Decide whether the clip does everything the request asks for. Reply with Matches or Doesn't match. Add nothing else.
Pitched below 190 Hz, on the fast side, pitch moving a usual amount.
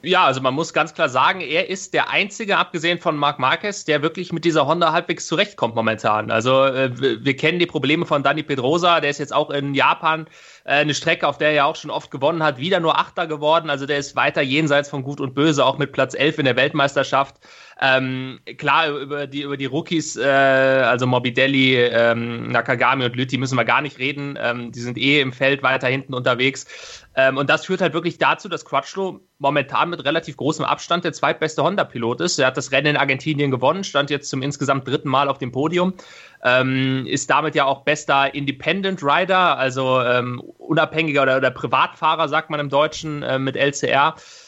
Matches